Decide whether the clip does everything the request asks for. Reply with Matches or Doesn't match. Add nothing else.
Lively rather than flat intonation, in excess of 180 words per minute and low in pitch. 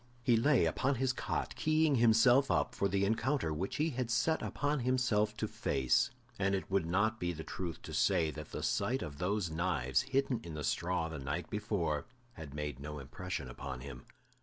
Matches